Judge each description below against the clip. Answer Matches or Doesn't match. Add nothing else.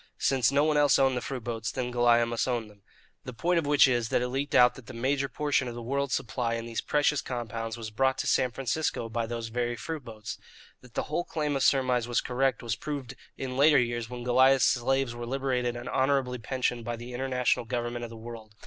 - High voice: Doesn't match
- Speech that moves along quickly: Matches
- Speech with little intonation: Matches